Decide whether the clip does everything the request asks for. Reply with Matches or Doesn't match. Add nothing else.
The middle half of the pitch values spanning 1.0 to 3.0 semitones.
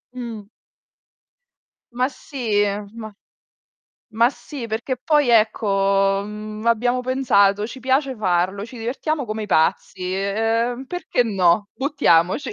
Doesn't match